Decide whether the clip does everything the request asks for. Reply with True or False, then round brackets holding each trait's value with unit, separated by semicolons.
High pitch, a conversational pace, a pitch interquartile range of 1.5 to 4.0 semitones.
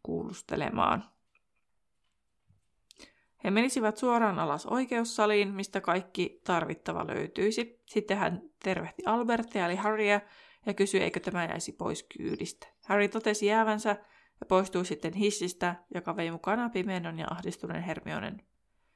True (200 Hz; 115 wpm; 3.6 semitones)